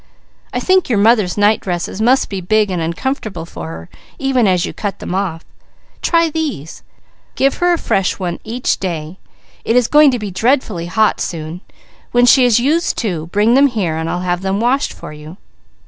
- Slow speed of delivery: No, average, 195 wpm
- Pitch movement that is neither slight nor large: No, wide, 6.2 semitones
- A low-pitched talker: No, high, 205 Hz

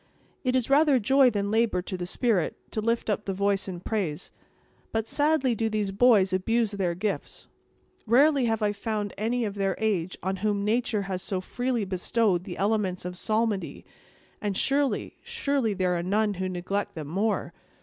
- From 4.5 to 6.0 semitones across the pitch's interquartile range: No, average, 3.5 semitones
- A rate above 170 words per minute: Yes, average, 180 wpm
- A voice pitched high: Yes, high, 210 Hz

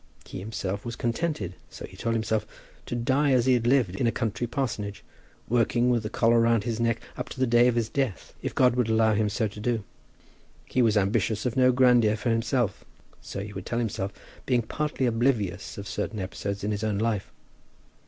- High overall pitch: No, low, 115 Hz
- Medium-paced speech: No, fast, 210 wpm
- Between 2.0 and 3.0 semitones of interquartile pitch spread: Yes, narrow, 2.5 semitones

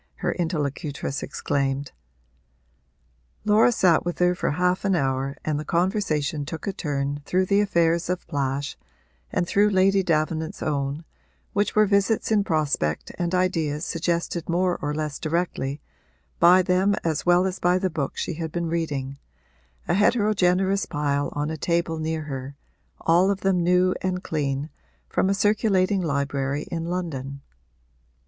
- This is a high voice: No, medium, 170 Hz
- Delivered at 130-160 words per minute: Yes, average, 150 wpm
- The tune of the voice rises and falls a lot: No, average, 4.1 semitones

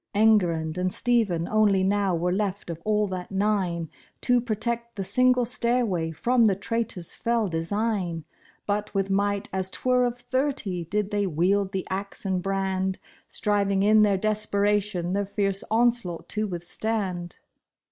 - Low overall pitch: No, high, 200 Hz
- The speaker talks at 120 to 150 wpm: Yes, average, 145 wpm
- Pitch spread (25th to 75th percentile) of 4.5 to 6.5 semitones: No, average, 2.8 semitones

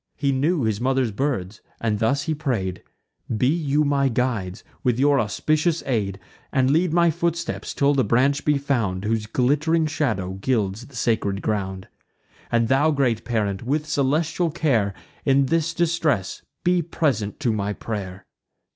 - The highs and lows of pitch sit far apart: Yes, wide, 5.9 semitones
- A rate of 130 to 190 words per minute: Yes, average, 155 wpm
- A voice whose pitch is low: Yes, low, 130 Hz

